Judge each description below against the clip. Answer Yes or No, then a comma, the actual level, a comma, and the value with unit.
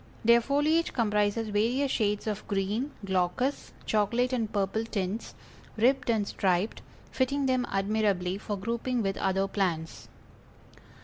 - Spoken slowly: Yes, slow, 125 wpm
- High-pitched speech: Yes, high, 215 Hz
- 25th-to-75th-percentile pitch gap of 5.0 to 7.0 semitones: No, average, 4.0 semitones